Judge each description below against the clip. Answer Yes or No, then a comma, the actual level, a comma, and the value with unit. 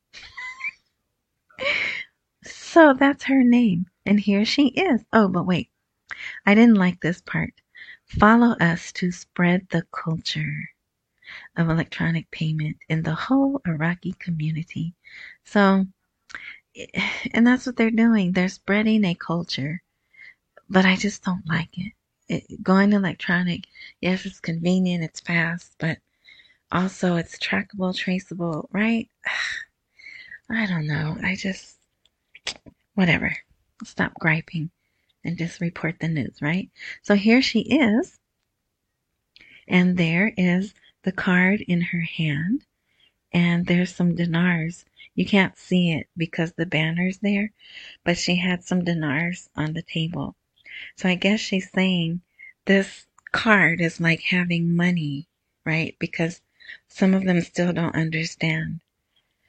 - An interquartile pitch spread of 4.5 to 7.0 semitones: No, average, 3.6 semitones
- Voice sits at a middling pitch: Yes, medium, 180 Hz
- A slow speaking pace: Yes, slow, 125 wpm